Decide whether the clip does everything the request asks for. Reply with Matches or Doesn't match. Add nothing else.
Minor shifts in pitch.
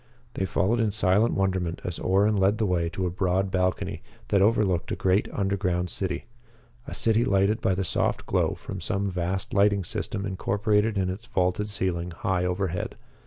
Matches